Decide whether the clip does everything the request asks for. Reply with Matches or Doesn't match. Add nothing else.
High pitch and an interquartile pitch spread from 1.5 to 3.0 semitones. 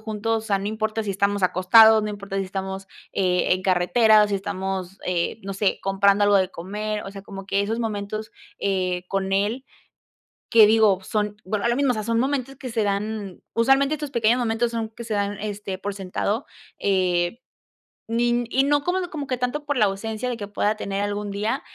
Matches